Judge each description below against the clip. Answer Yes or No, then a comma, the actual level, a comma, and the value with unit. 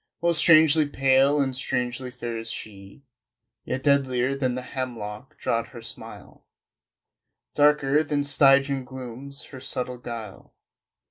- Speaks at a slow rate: Yes, slow, 125 wpm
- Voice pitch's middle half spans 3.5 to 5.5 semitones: No, narrow, 2.4 semitones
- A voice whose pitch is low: Yes, low, 130 Hz